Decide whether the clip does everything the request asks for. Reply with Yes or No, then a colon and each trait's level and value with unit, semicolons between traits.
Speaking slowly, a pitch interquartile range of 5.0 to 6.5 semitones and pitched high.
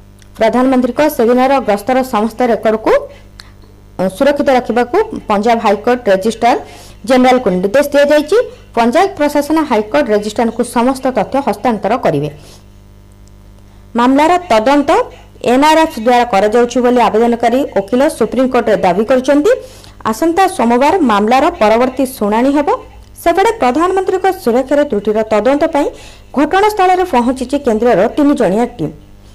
Yes: slow, 100 wpm; wide, 5.4 semitones; high, 245 Hz